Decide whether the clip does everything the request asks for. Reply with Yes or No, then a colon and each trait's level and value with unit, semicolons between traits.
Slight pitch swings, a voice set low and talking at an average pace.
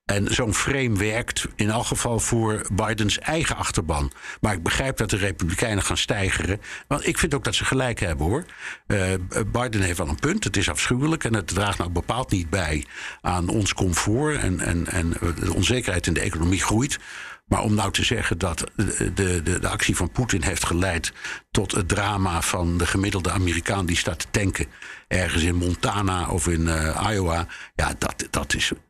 No: average, 3.7 semitones; low, 100 Hz; average, 190 wpm